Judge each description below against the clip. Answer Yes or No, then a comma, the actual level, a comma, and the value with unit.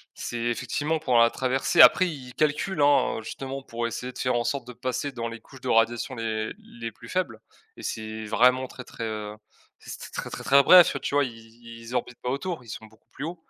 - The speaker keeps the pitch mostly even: No, average, 3.2 semitones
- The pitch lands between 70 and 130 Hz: Yes, low, 125 Hz